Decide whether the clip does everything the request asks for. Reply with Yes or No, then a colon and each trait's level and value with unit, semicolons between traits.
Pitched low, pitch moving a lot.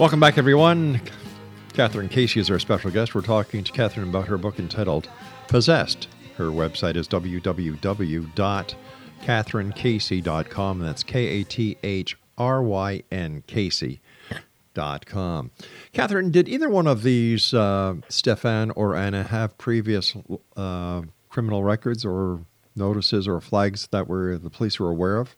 No: low, 100 Hz; average, 3.8 semitones